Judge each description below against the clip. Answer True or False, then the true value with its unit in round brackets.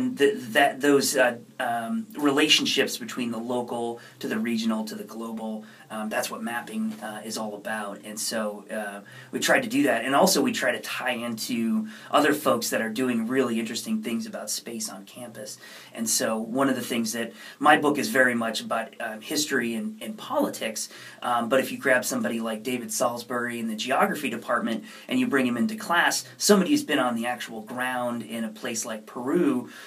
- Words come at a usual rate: True (195 wpm)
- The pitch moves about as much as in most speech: True (5.0 semitones)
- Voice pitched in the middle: False (120 Hz)